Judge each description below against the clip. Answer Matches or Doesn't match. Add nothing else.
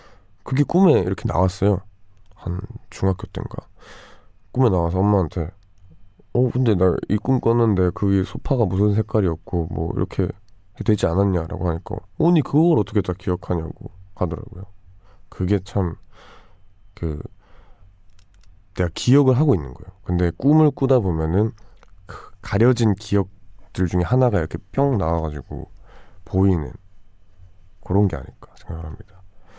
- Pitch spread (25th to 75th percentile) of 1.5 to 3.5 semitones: Matches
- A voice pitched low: Matches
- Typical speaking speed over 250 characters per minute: Matches